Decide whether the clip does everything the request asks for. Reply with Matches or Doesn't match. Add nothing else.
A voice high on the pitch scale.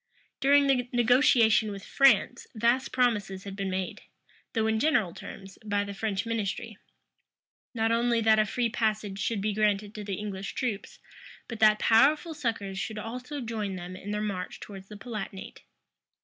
Matches